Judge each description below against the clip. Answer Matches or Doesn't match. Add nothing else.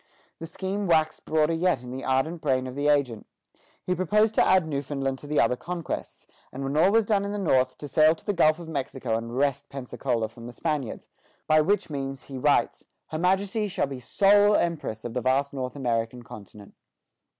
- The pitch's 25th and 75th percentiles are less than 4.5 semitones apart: Doesn't match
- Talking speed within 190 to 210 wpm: Matches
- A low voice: Doesn't match